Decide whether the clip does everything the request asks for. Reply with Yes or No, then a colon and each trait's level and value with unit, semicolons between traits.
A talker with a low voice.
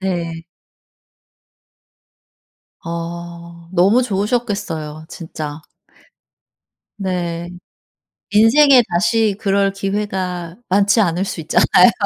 No: medium, 185 Hz